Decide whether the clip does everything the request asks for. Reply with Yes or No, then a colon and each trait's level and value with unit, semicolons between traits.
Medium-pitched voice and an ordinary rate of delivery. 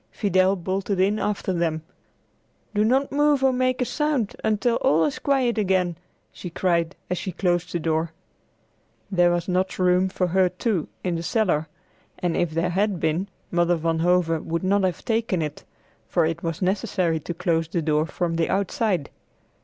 Yes: medium, 180 Hz; average, 175 wpm